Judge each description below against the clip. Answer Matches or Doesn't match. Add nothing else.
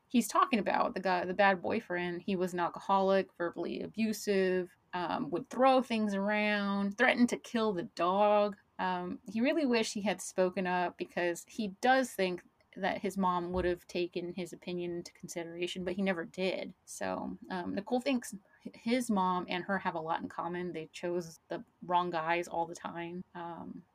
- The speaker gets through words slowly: Doesn't match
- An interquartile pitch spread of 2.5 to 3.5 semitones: Matches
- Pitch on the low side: Doesn't match